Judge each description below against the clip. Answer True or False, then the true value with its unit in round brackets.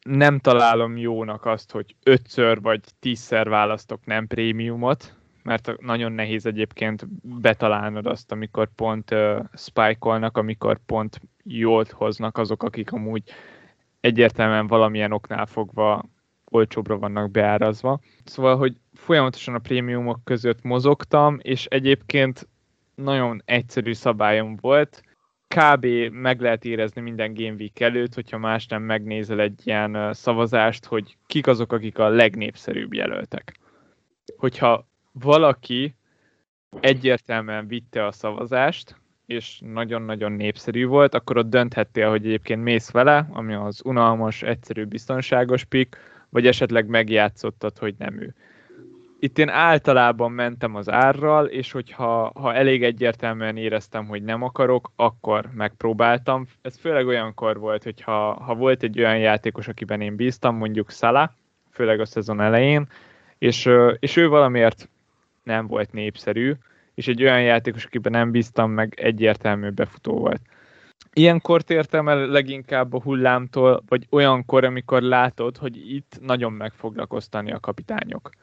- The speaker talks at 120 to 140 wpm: True (130 wpm)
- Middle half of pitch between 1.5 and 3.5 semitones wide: True (2.7 semitones)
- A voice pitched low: True (115 Hz)